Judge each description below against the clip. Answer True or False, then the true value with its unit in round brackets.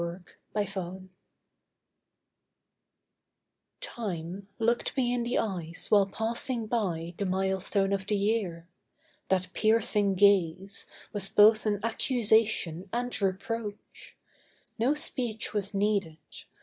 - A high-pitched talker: True (205 Hz)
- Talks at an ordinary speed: False (105 wpm)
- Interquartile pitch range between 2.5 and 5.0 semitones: True (2.9 semitones)